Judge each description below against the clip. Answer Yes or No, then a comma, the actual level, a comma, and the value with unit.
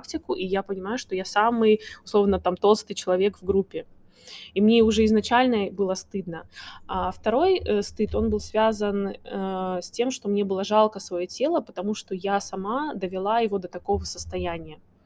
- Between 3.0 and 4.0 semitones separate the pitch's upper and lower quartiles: No, narrow, 2.6 semitones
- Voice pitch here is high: Yes, high, 200 Hz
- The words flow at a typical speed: No, fast, 175 wpm